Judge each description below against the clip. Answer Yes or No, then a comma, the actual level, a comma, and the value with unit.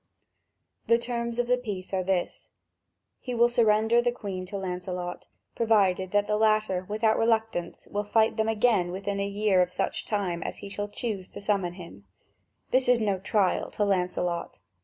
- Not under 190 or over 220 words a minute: No, average, 175 wpm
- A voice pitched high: Yes, high, 205 Hz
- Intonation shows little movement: No, average, 3.3 semitones